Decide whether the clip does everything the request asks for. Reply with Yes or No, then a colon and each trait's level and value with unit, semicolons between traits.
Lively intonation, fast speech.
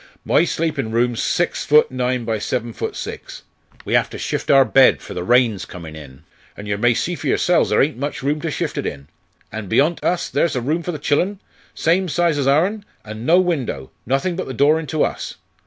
Yes: wide, 6.2 semitones; fast, 220 wpm